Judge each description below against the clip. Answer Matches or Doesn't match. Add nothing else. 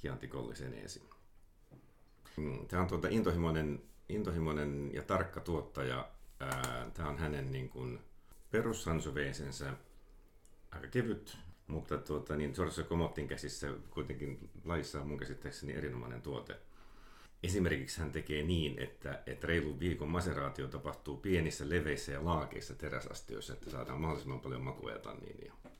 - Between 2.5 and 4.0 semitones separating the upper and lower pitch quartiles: Matches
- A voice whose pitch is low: Matches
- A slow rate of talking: Doesn't match